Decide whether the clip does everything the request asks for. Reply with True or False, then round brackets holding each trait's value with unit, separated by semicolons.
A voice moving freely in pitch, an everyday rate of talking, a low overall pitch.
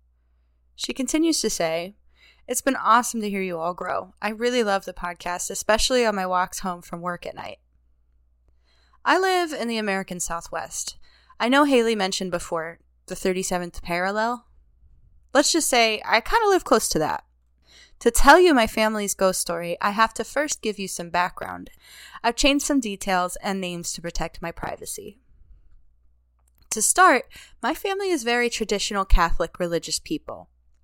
False (6.0 semitones; 165 wpm; 190 Hz)